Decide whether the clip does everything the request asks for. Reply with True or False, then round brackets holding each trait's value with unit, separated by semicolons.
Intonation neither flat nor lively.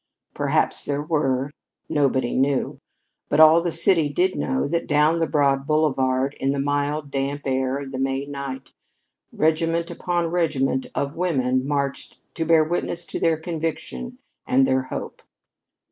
True (3.2 semitones)